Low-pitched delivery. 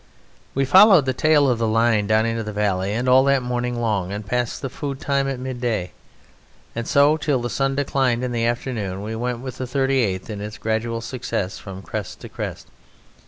Yes: low, 120 Hz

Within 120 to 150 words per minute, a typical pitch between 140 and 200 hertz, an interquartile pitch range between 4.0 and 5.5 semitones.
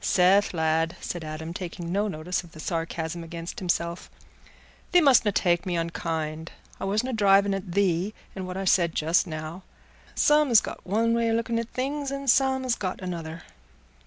No: average, 180 wpm; medium, 185 Hz; average, 4.8 semitones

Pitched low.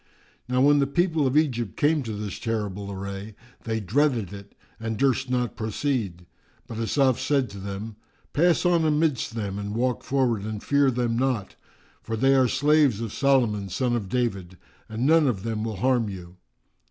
Yes: low, 115 Hz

